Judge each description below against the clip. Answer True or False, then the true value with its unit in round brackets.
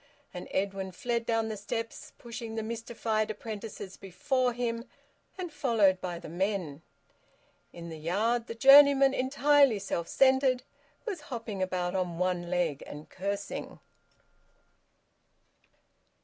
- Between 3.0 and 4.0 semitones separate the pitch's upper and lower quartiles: False (4.9 semitones)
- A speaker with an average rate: False (120 wpm)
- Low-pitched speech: False (220 Hz)